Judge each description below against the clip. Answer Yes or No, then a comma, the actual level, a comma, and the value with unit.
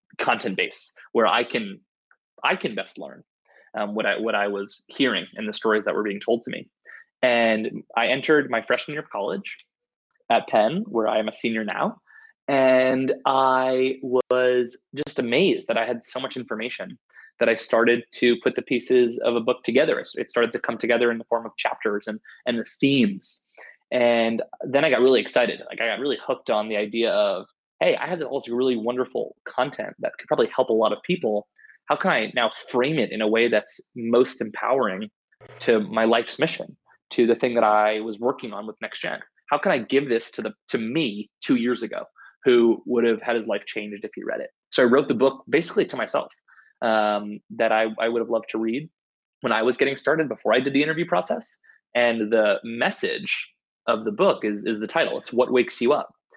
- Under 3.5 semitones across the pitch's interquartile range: Yes, average, 2.8 semitones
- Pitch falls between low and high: No, low, 120 Hz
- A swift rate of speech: Yes, fast, 215 wpm